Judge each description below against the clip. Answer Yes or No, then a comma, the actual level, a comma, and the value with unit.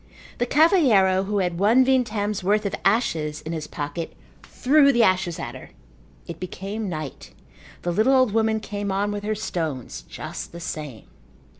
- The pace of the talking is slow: No, average, 165 wpm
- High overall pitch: Yes, high, 200 Hz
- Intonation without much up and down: No, average, 4.6 semitones